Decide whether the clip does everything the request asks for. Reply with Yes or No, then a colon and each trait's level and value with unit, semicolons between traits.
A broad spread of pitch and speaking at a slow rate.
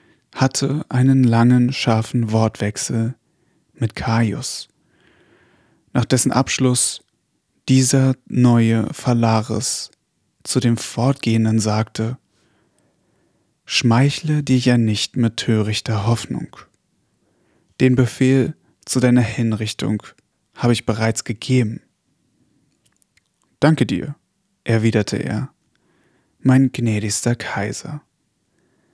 No: average, 2.8 semitones; slow, 85 wpm